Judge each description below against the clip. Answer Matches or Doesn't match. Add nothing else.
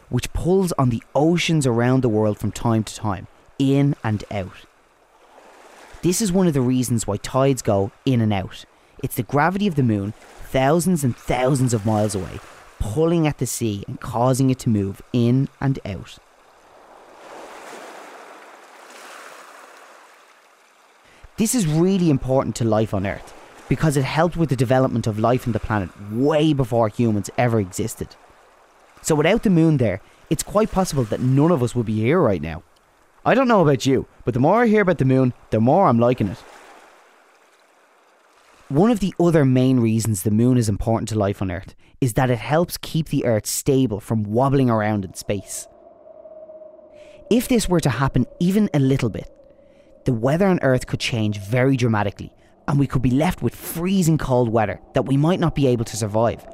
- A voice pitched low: Matches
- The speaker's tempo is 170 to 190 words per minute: Matches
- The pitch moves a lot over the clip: Matches